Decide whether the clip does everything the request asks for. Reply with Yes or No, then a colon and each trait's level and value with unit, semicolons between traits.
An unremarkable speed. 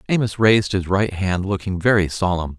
Yes: average, 185 wpm